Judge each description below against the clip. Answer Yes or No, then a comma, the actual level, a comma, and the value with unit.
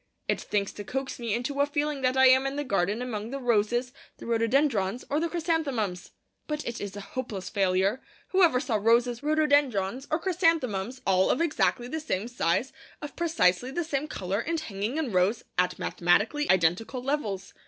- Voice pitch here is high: Yes, high, 245 Hz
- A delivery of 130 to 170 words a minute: No, average, 180 wpm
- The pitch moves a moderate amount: No, wide, 6.2 semitones